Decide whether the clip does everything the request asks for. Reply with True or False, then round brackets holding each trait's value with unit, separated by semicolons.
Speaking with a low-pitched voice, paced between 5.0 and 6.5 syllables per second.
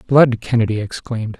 True (115 Hz; 5.7 syllables/s)